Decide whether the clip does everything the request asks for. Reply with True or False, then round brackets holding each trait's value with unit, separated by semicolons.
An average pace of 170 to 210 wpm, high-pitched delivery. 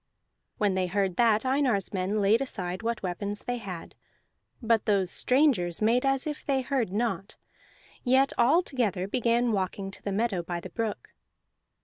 False (160 wpm; 215 Hz)